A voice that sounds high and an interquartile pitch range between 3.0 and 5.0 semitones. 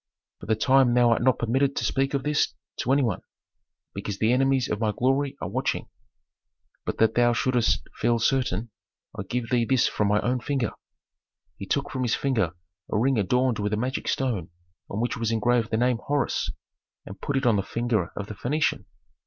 No: low, 120 Hz; average, 3.3 semitones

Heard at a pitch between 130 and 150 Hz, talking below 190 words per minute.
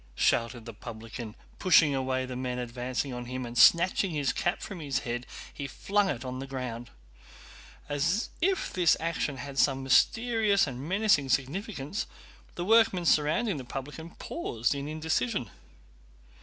Yes: medium, 140 Hz; average, 150 wpm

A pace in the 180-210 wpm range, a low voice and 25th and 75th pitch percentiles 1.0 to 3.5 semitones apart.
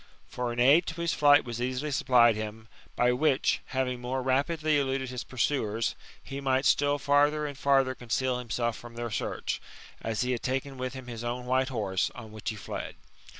Yes: average, 195 wpm; low, 130 Hz; narrow, 2.6 semitones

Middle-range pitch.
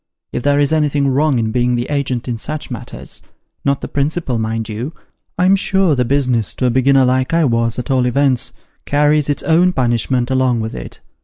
No: low, 130 Hz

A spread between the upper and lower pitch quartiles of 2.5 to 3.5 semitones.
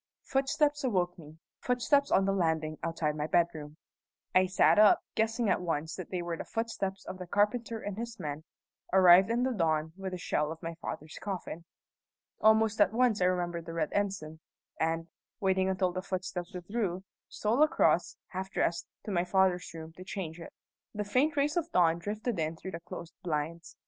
No: average, 4.3 semitones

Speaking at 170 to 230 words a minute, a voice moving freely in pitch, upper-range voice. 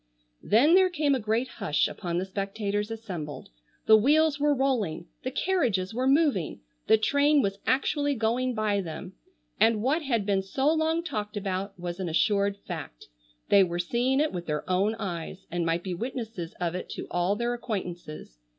Yes: average, 180 wpm; wide, 6.1 semitones; high, 210 Hz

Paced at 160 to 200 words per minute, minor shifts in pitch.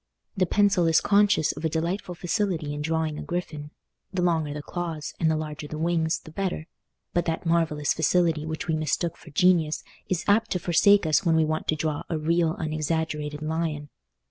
Yes: average, 190 wpm; narrow, 2.2 semitones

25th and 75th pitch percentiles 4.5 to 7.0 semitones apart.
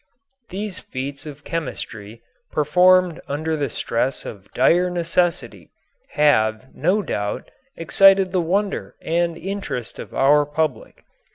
Yes: average, 5.3 semitones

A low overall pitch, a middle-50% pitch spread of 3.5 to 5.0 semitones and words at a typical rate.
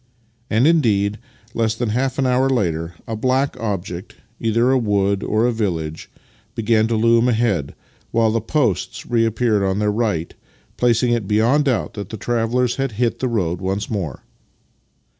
No: low, 115 Hz; average, 3.0 semitones; average, 175 wpm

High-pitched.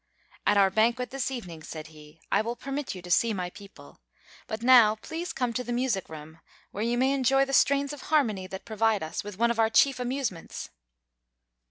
Yes: high, 230 Hz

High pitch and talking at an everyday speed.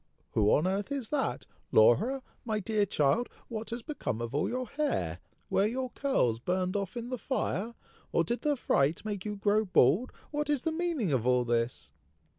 Yes: high, 210 Hz; average, 190 wpm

